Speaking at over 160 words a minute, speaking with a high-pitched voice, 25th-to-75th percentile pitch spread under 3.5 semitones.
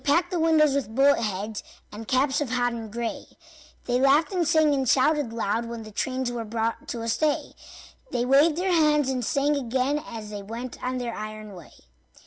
No: average, 200 wpm; very high, 255 Hz; average, 4.3 semitones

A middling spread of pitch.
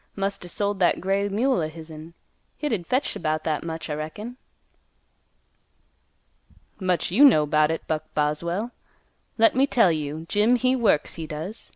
No: wide, 5.7 semitones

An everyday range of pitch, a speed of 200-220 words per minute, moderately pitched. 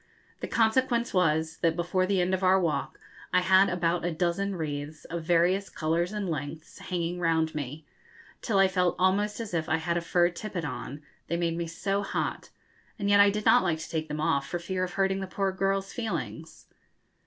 Yes: average, 3.1 semitones; fast, 205 wpm; medium, 175 Hz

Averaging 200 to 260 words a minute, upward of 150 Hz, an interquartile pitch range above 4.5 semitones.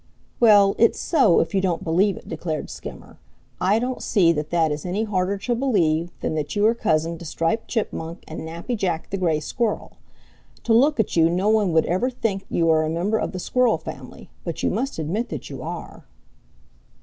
Yes: fast, 205 wpm; medium, 185 Hz; average, 5.1 semitones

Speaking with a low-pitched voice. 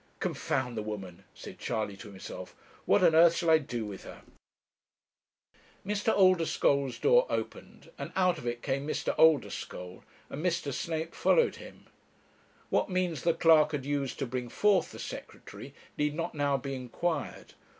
No: medium, 150 Hz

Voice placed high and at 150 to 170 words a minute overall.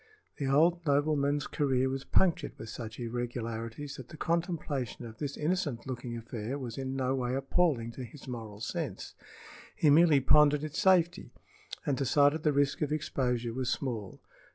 No: low, 135 Hz; average, 160 wpm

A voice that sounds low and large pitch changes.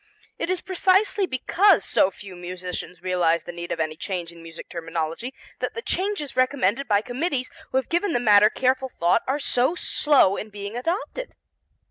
No: high, 240 Hz; wide, 8.7 semitones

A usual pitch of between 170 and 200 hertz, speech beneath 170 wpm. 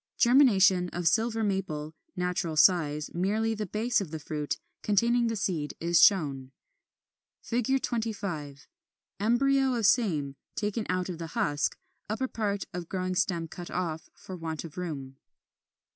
Yes: medium, 185 Hz; average, 140 wpm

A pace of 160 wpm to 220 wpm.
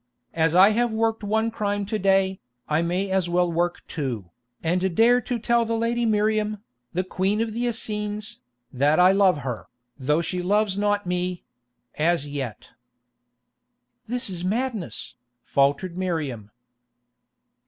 No: average, 140 wpm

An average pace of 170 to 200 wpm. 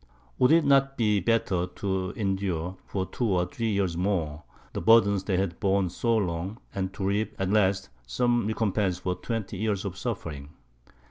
Yes: average, 175 wpm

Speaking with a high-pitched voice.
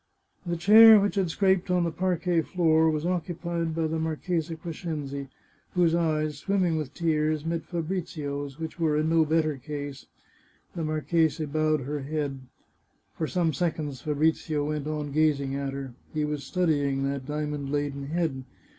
No: medium, 155 Hz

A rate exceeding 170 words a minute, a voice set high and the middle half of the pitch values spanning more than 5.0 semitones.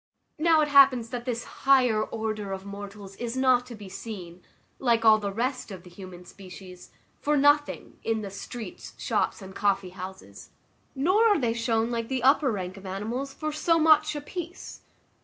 Yes: average, 180 wpm; high, 230 Hz; wide, 5.6 semitones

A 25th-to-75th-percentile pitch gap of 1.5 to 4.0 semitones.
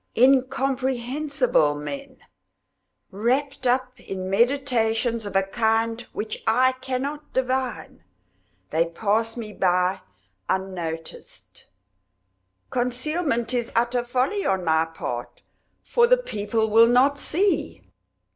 No: average, 4.4 semitones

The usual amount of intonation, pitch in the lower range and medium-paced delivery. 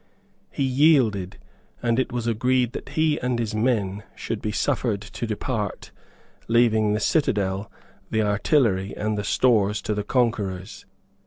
Yes: average, 3.4 semitones; low, 110 Hz; average, 145 wpm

